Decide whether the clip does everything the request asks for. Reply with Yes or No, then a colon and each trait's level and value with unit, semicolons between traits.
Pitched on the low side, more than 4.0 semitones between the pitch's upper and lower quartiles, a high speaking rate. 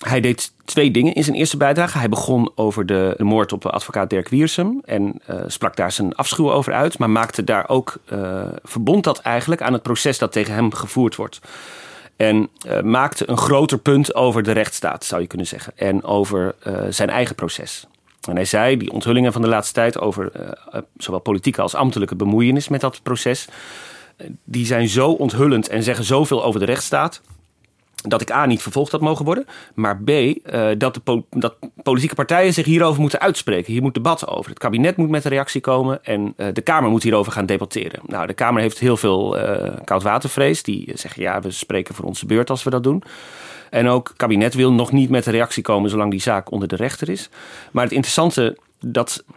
Yes: low, 120 Hz; average, 4.5 semitones; fast, 205 wpm